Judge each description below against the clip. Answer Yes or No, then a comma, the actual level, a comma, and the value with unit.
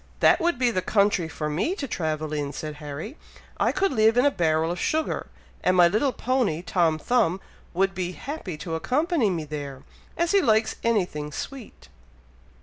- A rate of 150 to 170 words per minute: No, average, 185 wpm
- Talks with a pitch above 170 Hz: Yes, medium, 185 Hz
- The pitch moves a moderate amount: No, wide, 8.1 semitones